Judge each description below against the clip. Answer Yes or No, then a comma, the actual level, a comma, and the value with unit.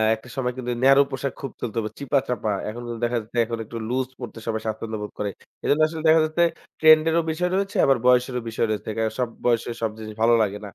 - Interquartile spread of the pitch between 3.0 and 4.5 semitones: Yes, average, 3.8 semitones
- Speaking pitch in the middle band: No, low, 125 Hz